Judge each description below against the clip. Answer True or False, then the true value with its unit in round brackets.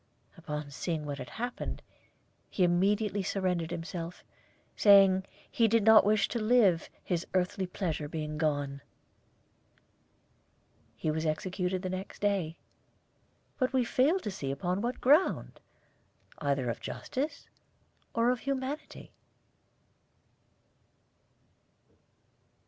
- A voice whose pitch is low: False (185 Hz)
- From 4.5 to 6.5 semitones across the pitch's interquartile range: True (5.6 semitones)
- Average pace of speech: False (110 wpm)